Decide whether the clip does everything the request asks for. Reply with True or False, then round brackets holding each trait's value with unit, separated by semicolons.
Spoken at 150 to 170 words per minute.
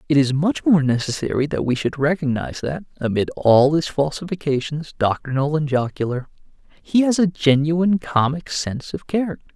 True (155 wpm)